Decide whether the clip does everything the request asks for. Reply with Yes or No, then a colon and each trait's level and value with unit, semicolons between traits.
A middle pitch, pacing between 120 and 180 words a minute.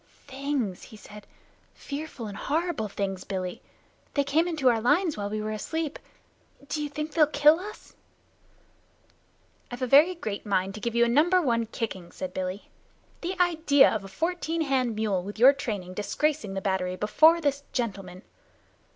No: very high, 250 Hz; average, 160 wpm